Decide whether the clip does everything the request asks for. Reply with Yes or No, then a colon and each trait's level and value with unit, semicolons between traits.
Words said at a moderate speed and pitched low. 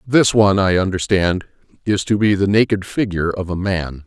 Yes: average, 190 wpm; very low, 95 Hz